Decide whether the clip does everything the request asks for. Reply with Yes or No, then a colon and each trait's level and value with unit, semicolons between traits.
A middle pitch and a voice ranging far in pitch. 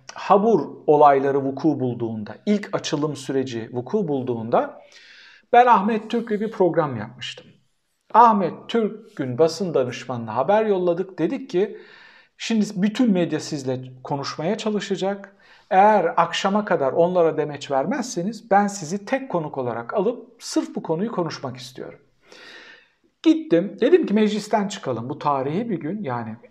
Yes: medium, 180 Hz; wide, 7.7 semitones